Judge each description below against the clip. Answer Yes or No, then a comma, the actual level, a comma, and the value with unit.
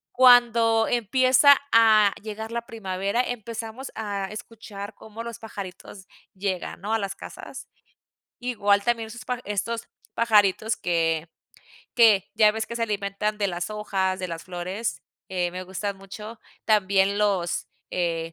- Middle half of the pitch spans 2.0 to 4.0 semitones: Yes, average, 3.0 semitones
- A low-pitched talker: No, high, 210 Hz